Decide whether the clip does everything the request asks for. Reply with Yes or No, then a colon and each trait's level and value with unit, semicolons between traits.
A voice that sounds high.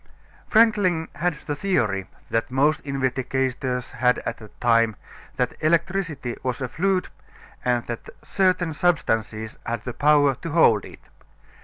No: low, 135 Hz